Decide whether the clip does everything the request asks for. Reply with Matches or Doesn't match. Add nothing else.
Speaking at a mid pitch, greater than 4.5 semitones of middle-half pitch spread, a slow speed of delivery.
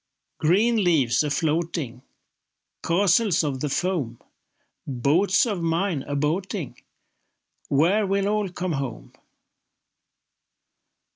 Matches